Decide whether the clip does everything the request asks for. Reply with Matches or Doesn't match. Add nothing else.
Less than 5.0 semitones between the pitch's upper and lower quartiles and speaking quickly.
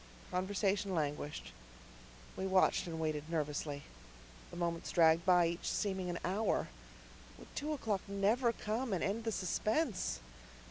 Doesn't match